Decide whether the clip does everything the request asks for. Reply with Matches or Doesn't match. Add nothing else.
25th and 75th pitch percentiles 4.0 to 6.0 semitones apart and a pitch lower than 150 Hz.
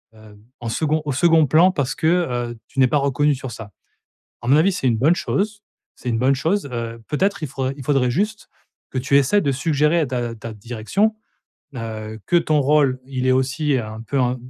Matches